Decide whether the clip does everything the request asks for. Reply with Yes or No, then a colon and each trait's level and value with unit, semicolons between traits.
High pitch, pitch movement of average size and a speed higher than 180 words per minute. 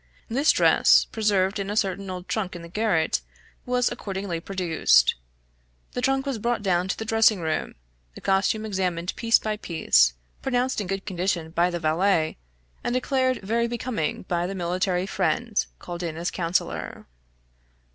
No: high, 195 Hz; average, 4.3 semitones; average, 160 wpm